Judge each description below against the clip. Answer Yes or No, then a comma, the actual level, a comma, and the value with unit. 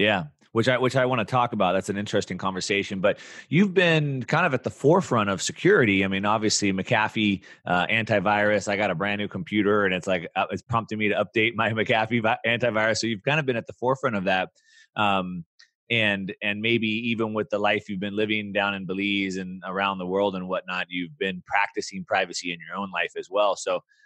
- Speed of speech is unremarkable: No, fast, 215 wpm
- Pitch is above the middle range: No, low, 105 Hz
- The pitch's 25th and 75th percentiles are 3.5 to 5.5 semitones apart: No, average, 2.9 semitones